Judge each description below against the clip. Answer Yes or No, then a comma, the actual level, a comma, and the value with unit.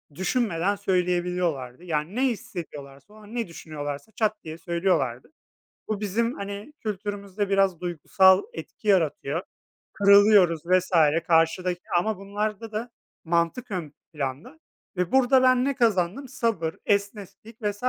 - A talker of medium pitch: No, high, 195 Hz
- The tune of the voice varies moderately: Yes, average, 4.2 semitones